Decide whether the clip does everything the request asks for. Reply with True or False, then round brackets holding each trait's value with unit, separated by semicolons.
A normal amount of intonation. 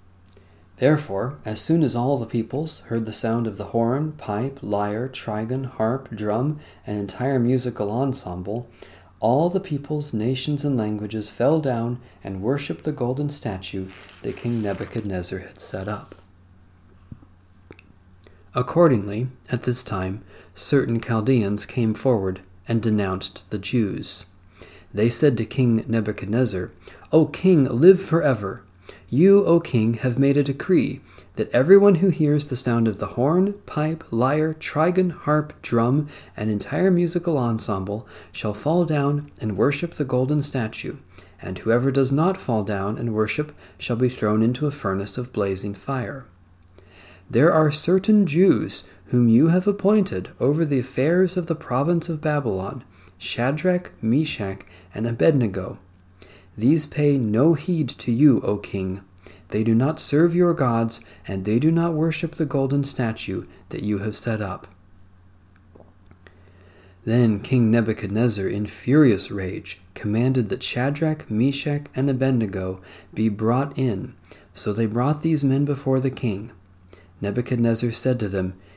False (6.3 semitones)